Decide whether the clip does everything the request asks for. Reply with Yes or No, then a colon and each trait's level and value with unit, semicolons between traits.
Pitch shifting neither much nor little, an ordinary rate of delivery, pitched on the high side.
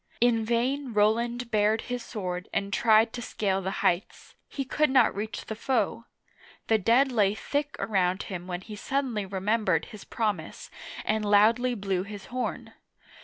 Yes: average, 3.2 semitones; average, 160 wpm; high, 220 Hz